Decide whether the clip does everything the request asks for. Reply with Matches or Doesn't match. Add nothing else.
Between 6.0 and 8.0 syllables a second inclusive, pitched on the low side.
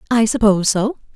Doesn't match